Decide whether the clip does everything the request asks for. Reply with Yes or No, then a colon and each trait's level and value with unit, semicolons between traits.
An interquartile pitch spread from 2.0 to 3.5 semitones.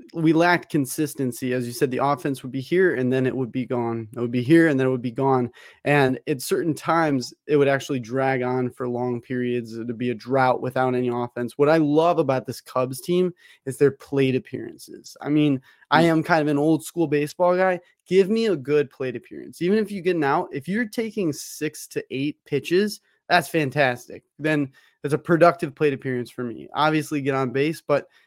No: average, 4.1 semitones